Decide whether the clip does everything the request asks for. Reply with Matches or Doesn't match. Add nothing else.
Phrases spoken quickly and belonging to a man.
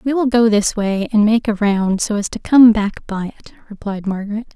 Doesn't match